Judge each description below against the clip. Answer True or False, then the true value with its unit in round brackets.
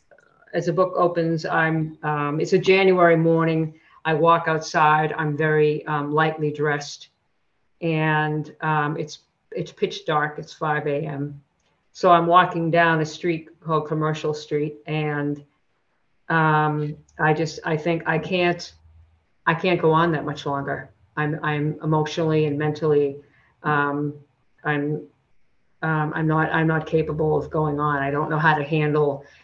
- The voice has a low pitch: False (155 Hz)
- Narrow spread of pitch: True (1.4 semitones)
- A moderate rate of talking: True (150 wpm)